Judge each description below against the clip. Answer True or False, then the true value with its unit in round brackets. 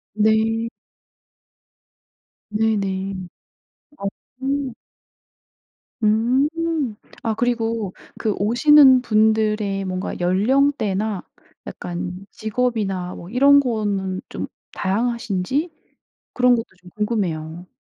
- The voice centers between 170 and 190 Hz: False (215 Hz)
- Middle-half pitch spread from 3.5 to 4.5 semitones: True (4.0 semitones)